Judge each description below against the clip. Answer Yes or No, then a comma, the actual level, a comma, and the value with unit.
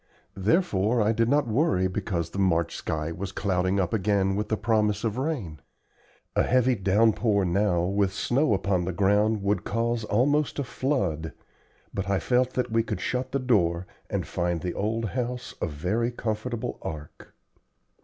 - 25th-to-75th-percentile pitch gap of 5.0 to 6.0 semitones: No, average, 4.3 semitones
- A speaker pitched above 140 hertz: No, low, 105 Hz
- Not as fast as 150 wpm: No, average, 170 wpm